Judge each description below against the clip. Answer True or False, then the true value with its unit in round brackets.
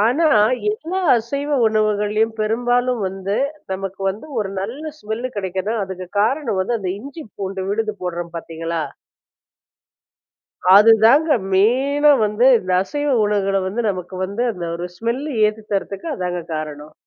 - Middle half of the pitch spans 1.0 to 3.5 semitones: False (4.3 semitones)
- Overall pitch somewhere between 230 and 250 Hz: False (210 Hz)